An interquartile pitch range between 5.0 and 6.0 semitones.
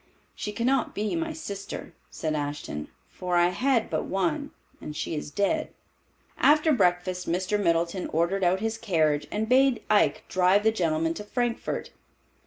Yes: average, 5.3 semitones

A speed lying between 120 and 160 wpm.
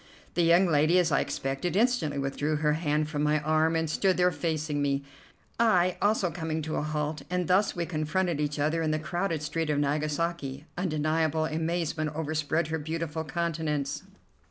No: average, 175 wpm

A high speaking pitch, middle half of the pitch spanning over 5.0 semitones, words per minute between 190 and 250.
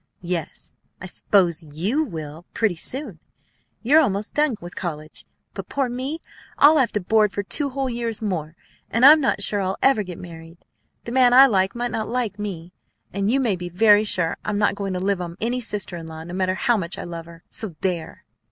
Yes: high, 200 Hz; wide, 5.5 semitones; fast, 205 wpm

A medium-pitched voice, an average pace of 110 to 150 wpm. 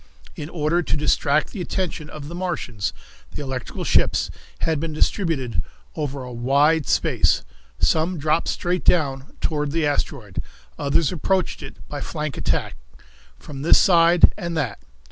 Yes: medium, 155 Hz; average, 145 wpm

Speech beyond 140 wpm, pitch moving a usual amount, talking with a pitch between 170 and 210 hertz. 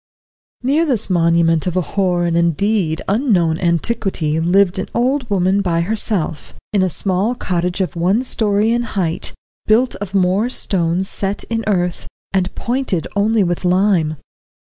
Yes: average, 150 wpm; average, 3.9 semitones; high, 190 Hz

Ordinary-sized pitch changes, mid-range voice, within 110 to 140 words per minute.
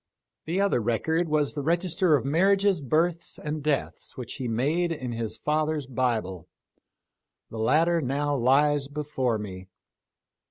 Yes: average, 4.6 semitones; medium, 145 Hz; slow, 135 wpm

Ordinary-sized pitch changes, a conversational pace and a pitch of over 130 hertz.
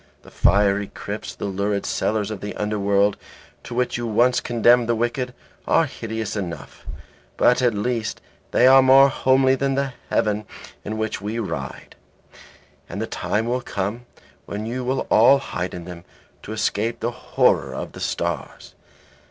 No: average, 3.3 semitones; average, 160 wpm; low, 110 Hz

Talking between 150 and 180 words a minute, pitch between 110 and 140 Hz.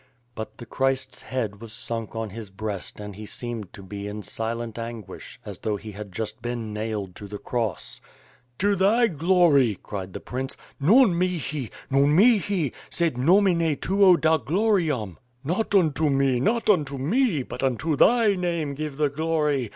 Yes: average, 165 wpm; low, 135 Hz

